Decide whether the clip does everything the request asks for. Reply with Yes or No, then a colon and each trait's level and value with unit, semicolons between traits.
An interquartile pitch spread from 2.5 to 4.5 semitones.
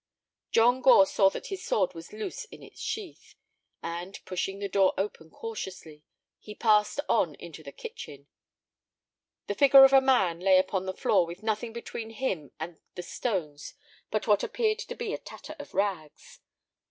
No: wide, 5.4 semitones